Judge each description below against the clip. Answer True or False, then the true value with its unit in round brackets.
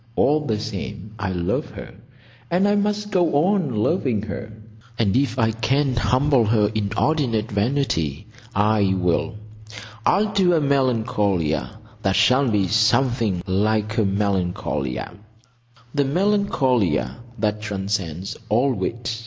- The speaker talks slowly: True (120 wpm)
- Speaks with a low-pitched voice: True (110 Hz)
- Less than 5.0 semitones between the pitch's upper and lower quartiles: False (5.3 semitones)